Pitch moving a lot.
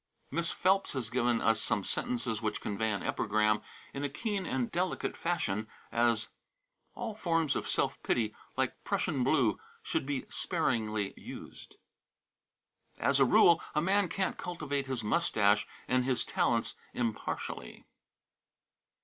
Yes: wide, 7.1 semitones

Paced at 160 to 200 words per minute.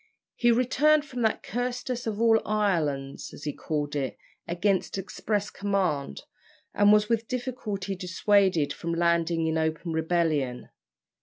No: slow, 135 wpm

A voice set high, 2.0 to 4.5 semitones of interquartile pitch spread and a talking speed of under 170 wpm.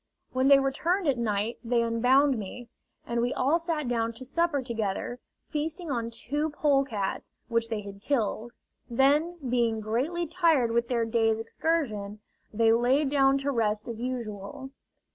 Yes: high, 245 Hz; average, 3.9 semitones; average, 155 wpm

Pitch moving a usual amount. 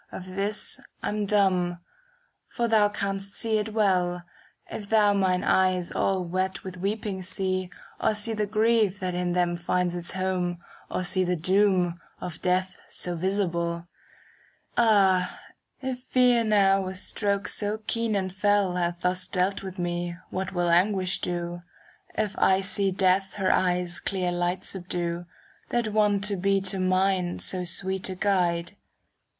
No: narrow, 2.2 semitones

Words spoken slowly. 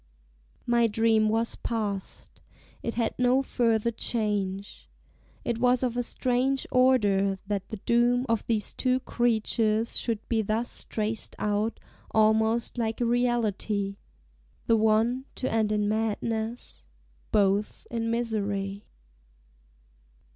Yes: slow, 120 wpm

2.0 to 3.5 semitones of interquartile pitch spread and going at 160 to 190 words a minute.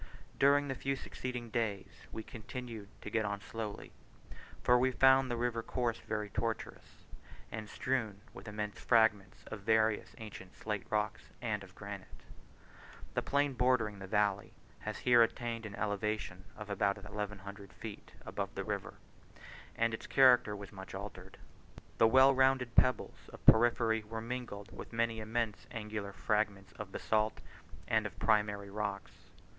No: average, 2.7 semitones; average, 150 wpm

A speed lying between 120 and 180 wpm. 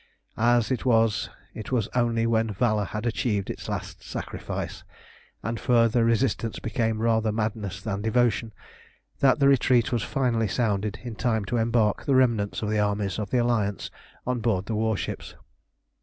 Yes: average, 160 wpm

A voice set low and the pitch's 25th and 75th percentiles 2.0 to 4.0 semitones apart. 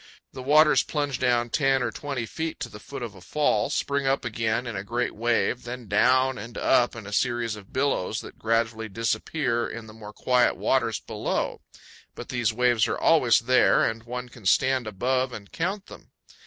Yes: low, 120 Hz; average, 2.8 semitones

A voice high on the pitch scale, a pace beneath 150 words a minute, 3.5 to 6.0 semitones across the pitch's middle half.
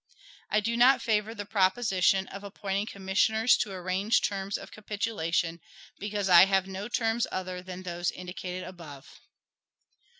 No: high, 195 Hz; average, 140 wpm; narrow, 2.6 semitones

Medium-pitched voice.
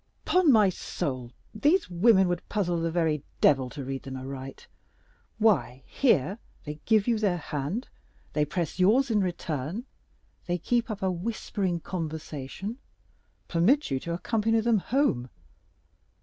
Yes: medium, 180 Hz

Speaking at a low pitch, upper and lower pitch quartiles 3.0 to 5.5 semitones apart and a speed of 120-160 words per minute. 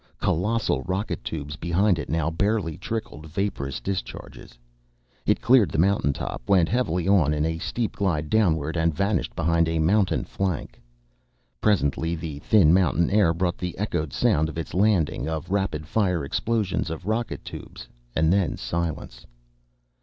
Yes: very low, 85 Hz; average, 4.1 semitones; average, 155 wpm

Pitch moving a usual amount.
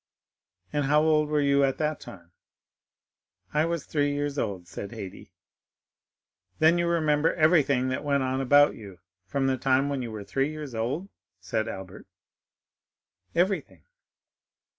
Yes: average, 3.5 semitones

